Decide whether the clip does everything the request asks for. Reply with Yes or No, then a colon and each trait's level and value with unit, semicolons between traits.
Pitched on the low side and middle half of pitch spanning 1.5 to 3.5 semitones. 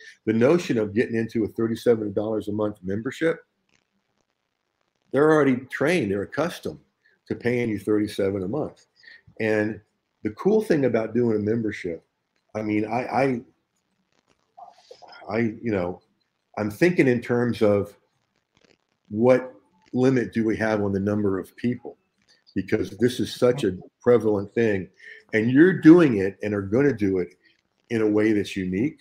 Yes: low, 110 Hz; average, 2.8 semitones